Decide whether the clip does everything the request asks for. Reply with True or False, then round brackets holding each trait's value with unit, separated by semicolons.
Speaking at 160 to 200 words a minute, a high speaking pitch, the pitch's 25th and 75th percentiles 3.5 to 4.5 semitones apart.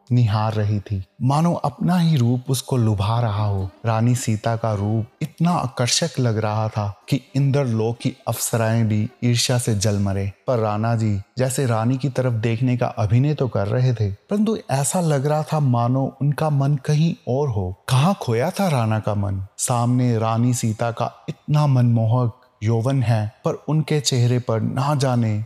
False (170 wpm; 120 Hz; 3.9 semitones)